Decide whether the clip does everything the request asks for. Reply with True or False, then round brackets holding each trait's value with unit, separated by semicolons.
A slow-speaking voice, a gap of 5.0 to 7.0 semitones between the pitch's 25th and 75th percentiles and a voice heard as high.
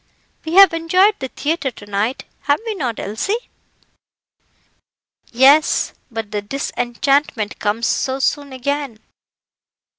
True (115 wpm; 5.5 semitones; 270 Hz)